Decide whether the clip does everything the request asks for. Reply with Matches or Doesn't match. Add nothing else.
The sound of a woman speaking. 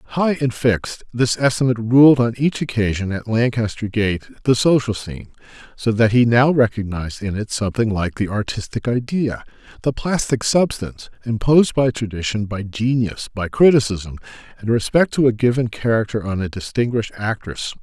Doesn't match